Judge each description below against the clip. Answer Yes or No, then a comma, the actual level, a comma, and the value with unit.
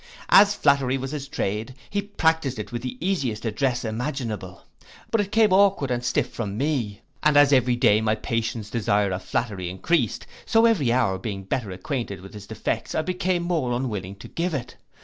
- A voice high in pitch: No, low, 125 Hz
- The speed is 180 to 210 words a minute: Yes, average, 190 wpm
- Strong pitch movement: Yes, wide, 6.1 semitones